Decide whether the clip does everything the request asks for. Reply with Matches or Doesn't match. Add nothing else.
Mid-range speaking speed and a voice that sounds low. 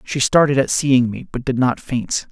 Doesn't match